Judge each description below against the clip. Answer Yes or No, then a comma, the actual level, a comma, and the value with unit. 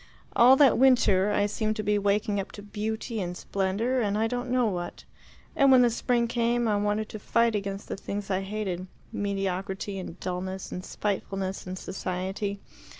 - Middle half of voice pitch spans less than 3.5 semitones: Yes, average, 3.1 semitones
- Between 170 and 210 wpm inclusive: Yes, average, 180 wpm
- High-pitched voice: Yes, high, 205 Hz